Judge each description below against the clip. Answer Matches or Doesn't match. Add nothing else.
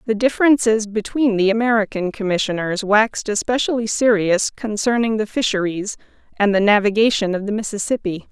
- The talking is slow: Matches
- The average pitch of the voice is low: Doesn't match